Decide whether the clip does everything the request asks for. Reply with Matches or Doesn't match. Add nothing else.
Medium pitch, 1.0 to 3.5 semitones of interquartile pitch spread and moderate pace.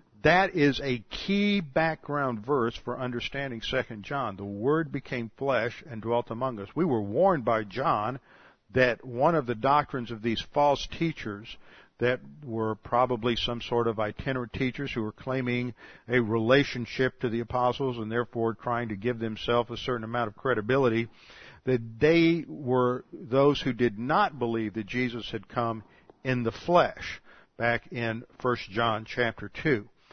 Doesn't match